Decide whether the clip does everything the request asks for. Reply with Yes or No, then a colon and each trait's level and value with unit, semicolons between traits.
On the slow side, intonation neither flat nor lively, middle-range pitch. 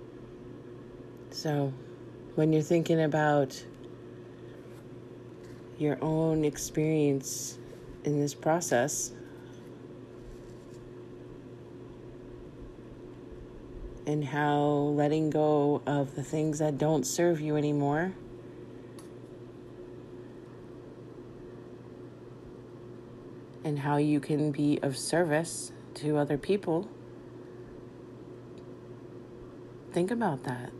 Yes: slow, 70 wpm; average, 3.7 semitones; medium, 145 Hz